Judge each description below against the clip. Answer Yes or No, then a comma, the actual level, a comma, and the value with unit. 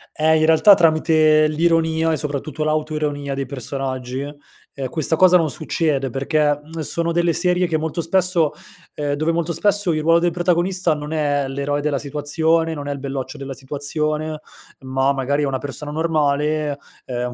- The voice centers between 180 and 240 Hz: No, medium, 155 Hz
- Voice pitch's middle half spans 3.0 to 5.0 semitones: No, narrow, 2.5 semitones